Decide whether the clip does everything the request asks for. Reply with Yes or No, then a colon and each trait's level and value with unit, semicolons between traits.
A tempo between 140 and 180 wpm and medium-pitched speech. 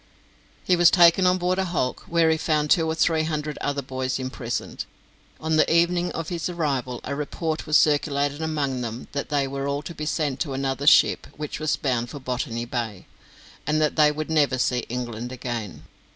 No: average, 195 wpm; medium, 145 Hz